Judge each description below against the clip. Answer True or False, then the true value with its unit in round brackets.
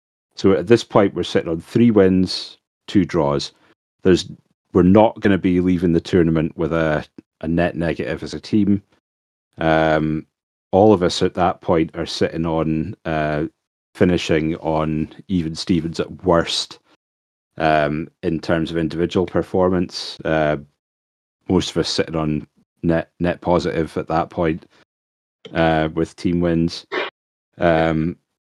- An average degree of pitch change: False (2.2 semitones)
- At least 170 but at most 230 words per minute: False (145 wpm)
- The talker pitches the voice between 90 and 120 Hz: False (80 Hz)